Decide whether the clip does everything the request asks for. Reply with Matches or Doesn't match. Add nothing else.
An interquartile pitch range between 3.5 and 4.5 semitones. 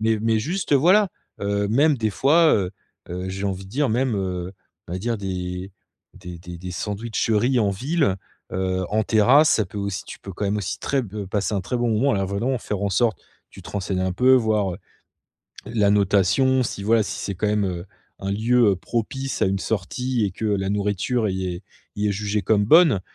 Matches